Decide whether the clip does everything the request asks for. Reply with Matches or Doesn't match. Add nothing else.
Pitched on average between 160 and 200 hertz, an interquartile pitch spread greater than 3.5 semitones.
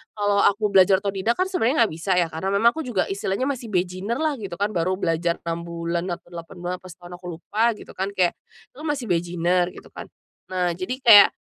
Matches